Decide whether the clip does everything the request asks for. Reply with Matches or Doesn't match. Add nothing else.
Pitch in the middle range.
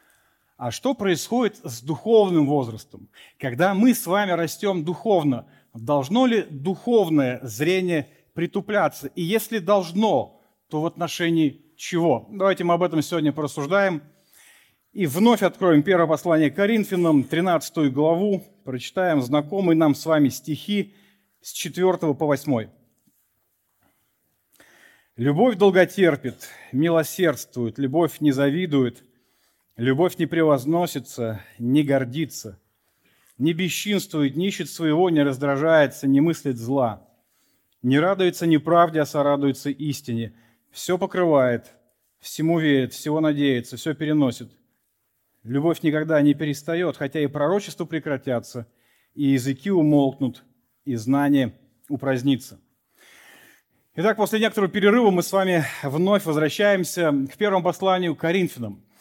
Matches